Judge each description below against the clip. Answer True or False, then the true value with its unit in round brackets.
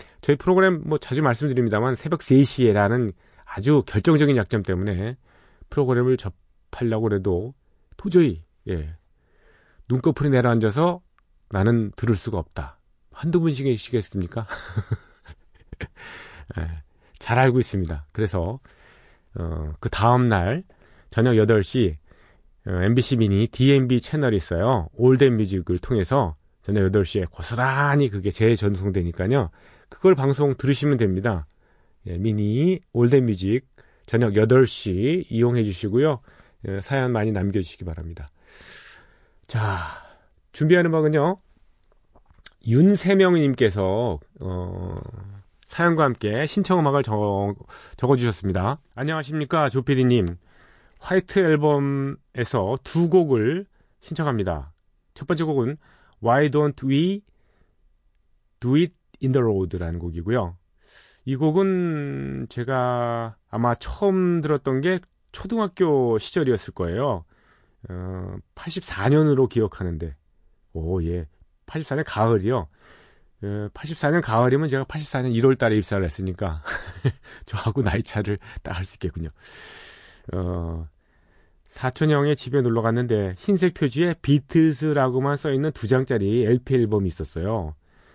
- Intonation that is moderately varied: False (7.0 semitones)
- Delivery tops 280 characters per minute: False (260 characters per minute)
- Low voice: True (115 Hz)